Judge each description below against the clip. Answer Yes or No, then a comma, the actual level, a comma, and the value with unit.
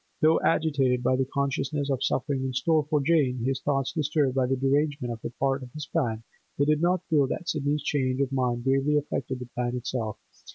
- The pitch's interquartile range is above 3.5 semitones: No, narrow, 2.6 semitones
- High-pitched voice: No, low, 135 Hz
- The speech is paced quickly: Yes, fast, 210 wpm